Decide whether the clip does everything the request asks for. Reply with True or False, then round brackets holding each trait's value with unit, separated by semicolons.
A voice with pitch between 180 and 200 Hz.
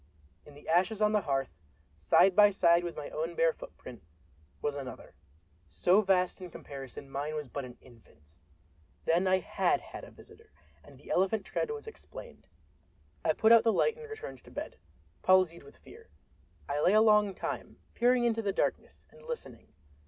True (185 Hz)